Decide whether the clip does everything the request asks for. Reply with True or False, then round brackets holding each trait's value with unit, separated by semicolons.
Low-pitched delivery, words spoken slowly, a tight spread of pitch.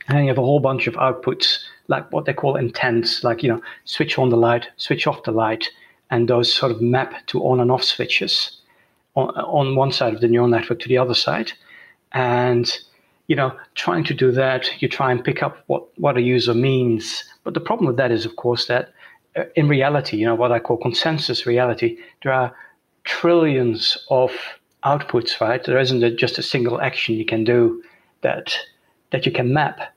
False (125 Hz; 205 wpm; 2.1 semitones)